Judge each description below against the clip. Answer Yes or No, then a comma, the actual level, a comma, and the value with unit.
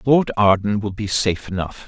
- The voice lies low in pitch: Yes, low, 105 Hz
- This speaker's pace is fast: No, average, 190 wpm